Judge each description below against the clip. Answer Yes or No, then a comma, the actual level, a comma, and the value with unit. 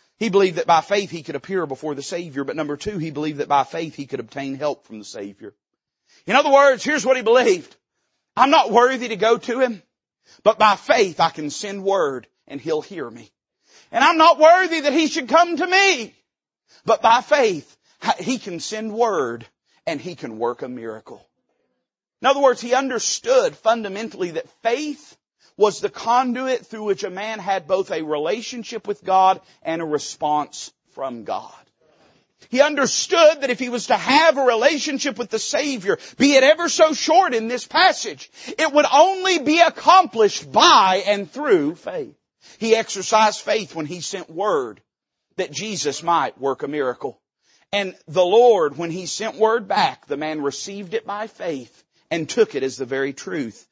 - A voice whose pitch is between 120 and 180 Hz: No, high, 220 Hz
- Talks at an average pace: Yes, average, 185 wpm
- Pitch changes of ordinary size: No, wide, 8.6 semitones